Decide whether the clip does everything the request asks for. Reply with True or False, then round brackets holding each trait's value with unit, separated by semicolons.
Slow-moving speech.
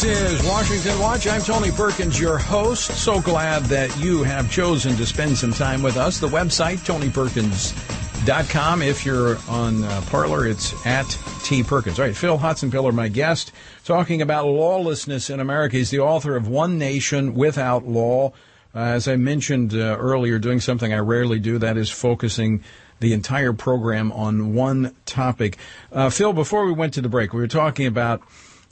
False (175 wpm)